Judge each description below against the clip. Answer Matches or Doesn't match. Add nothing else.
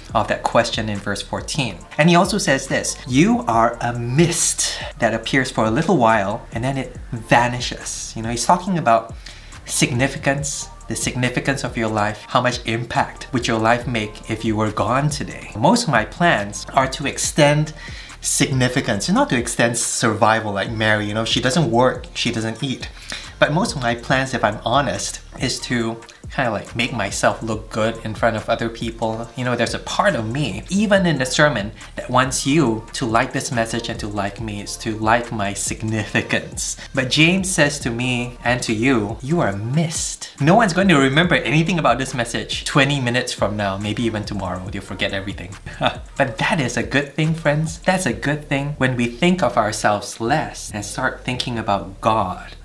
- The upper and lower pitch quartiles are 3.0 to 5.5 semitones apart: Matches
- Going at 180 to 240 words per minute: Matches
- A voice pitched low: Matches